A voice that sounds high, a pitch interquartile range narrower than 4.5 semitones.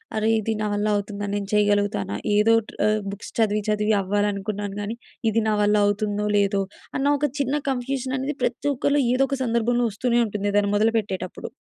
Yes: high, 210 Hz; narrow, 2.4 semitones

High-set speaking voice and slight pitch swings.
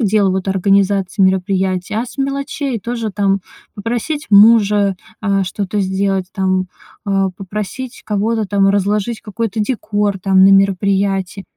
Yes: high, 200 Hz; narrow, 2.0 semitones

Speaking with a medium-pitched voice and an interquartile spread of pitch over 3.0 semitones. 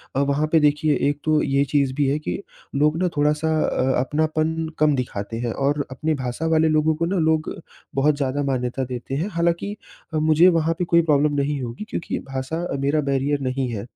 No: medium, 150 Hz; narrow, 2.6 semitones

